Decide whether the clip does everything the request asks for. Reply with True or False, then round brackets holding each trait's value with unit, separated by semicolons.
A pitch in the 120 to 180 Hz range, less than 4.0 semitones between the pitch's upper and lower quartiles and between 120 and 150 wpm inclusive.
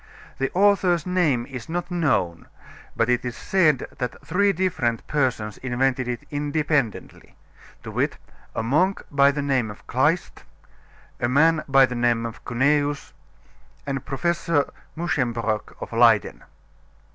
False (140 Hz; 4.9 semitones; 135 wpm)